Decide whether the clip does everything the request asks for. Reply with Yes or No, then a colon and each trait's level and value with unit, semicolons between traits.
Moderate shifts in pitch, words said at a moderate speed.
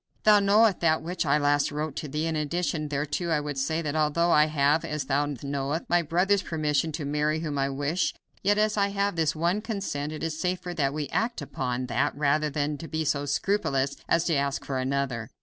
No: average, 3.1 semitones; fast, 220 wpm